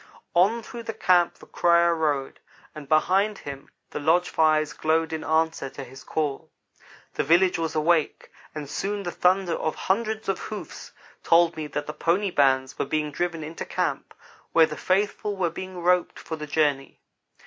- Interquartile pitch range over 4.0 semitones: No, average, 3.2 semitones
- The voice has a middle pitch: Yes, medium, 165 Hz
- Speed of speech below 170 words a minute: No, average, 175 wpm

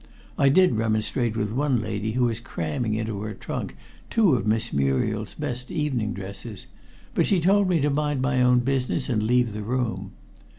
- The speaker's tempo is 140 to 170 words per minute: No, average, 180 wpm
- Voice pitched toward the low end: Yes, low, 120 Hz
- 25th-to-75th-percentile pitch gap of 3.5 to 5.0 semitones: Yes, average, 4.0 semitones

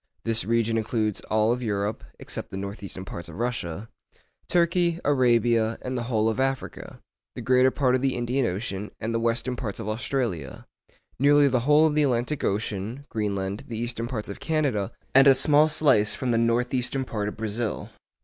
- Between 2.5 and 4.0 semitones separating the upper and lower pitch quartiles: Yes, average, 3.6 semitones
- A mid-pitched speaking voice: No, low, 120 Hz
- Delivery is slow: No, average, 185 wpm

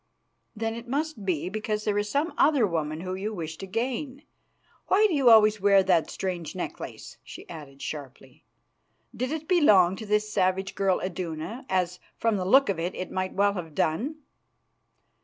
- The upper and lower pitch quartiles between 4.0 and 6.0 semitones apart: Yes, average, 4.6 semitones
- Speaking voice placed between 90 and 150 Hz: No, high, 200 Hz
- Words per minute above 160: Yes, average, 175 wpm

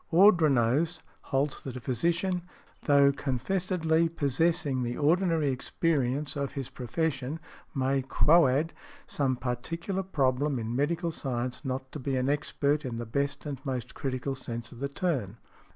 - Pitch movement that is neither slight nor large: Yes, average, 4.0 semitones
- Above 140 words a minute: No, slow, 135 wpm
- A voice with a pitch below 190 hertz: Yes, medium, 140 Hz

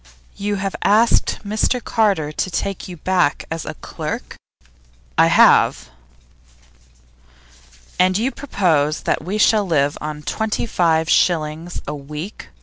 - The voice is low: No, medium, 180 Hz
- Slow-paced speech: Yes, slow, 130 wpm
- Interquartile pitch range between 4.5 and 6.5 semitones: Yes, average, 5.2 semitones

